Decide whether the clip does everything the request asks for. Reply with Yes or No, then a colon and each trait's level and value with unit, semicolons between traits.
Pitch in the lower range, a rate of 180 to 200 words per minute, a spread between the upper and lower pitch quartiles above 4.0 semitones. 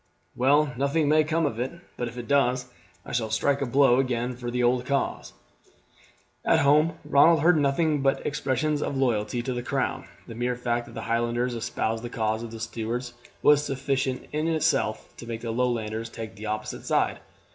No: low, 125 Hz; average, 190 wpm; average, 3.3 semitones